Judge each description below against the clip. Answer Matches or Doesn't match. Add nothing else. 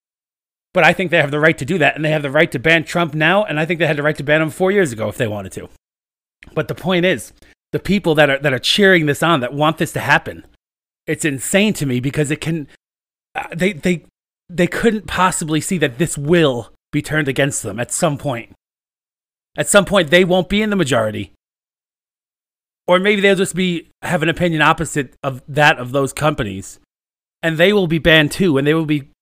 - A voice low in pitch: Doesn't match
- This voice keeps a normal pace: Doesn't match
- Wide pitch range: Doesn't match